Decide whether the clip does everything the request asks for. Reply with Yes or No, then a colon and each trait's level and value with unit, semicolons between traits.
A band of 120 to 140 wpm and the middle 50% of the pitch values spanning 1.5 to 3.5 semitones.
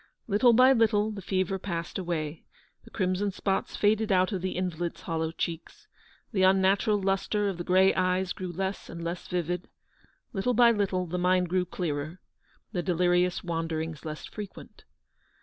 No: average, 165 wpm; narrow, 2.5 semitones